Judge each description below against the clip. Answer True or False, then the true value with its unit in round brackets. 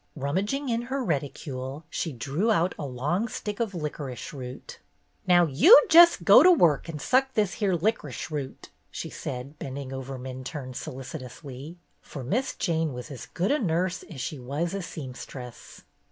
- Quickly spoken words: False (165 wpm)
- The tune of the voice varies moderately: False (6.8 semitones)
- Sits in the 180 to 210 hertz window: False (155 Hz)